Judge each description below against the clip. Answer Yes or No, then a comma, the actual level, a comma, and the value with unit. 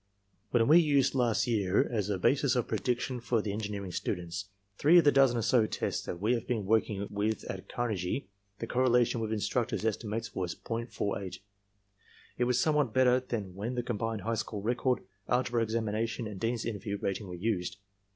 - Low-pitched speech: Yes, low, 115 Hz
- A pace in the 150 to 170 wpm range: No, average, 185 wpm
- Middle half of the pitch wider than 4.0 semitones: No, average, 3.2 semitones